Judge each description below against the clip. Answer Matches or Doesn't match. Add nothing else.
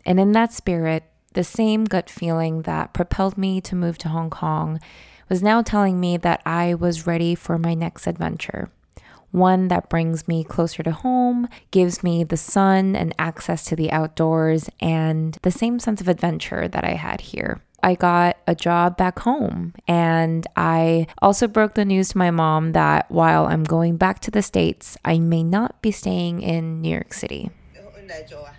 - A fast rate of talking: Doesn't match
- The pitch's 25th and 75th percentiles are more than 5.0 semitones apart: Doesn't match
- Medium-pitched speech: Matches